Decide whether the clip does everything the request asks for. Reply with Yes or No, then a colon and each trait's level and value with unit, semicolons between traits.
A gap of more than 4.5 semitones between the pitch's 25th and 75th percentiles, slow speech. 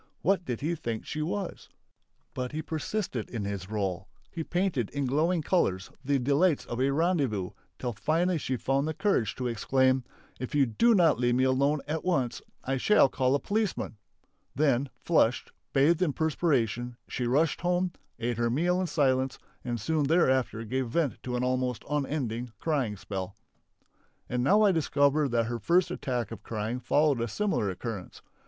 No: average, 5.0 semitones; average, 170 wpm